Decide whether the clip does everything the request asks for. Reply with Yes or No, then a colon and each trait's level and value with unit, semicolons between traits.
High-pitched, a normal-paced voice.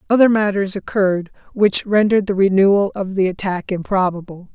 Yes: high, 195 Hz; average, 145 wpm